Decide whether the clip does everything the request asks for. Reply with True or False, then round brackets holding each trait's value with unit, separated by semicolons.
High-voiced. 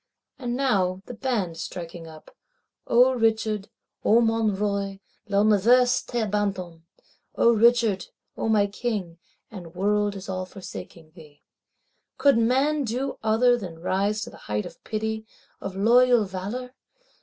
True (210 Hz)